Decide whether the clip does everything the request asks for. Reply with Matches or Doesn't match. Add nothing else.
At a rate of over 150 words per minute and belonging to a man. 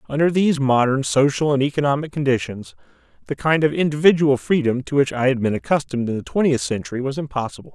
Matches